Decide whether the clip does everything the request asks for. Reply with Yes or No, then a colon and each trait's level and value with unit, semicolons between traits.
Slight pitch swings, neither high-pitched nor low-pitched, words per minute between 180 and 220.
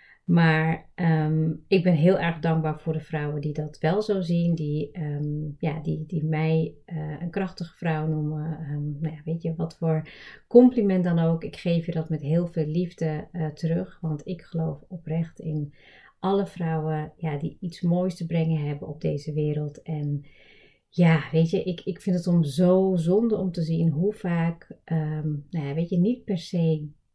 Yes: narrow, 2.2 semitones; medium, 160 Hz; average, 190 wpm